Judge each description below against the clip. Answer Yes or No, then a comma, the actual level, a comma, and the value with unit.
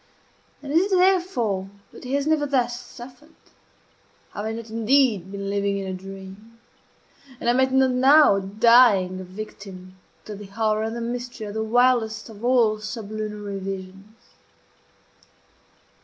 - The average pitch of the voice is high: Yes, high, 220 Hz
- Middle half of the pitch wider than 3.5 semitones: Yes, average, 4.0 semitones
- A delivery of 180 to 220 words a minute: No, average, 150 wpm